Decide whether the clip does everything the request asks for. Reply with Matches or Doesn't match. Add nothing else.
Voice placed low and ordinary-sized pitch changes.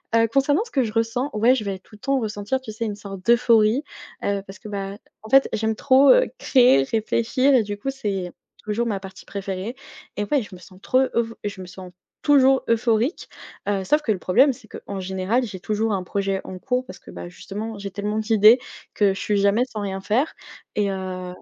Doesn't match